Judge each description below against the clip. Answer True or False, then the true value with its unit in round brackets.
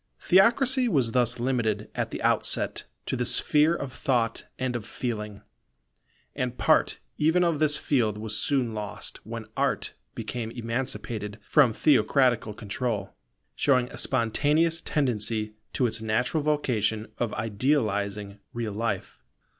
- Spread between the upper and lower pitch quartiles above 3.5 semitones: True (4.7 semitones)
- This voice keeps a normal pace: False (130 wpm)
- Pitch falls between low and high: False (120 Hz)